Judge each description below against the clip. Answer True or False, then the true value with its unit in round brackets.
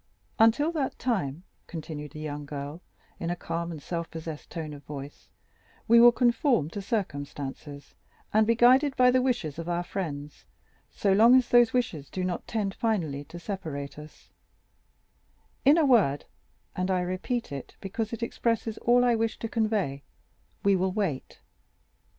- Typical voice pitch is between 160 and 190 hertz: True (185 Hz)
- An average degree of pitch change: False (7.4 semitones)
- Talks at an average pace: True (160 wpm)